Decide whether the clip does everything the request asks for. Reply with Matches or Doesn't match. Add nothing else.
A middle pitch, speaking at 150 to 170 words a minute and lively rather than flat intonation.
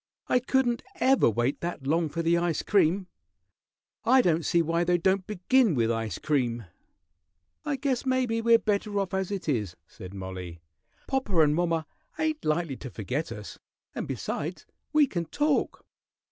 Matches